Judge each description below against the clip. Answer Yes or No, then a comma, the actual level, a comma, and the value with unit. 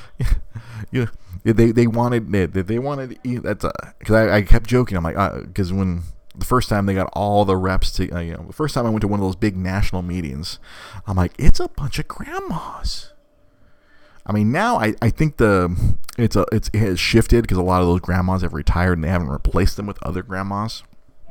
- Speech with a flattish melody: No, average, 3.9 semitones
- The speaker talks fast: Yes, fast, 215 wpm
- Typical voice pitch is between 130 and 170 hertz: No, low, 100 Hz